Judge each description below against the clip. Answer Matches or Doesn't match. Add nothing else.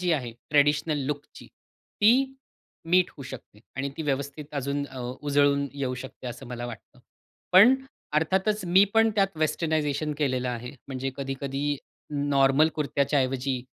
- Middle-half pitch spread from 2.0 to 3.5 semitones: Matches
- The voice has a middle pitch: Matches